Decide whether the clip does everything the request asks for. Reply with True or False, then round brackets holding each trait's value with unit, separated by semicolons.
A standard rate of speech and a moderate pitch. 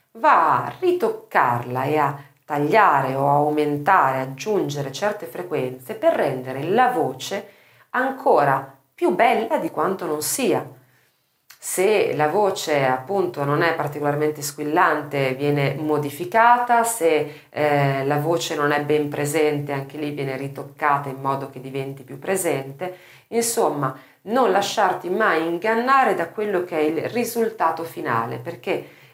True (130 wpm; 150 Hz)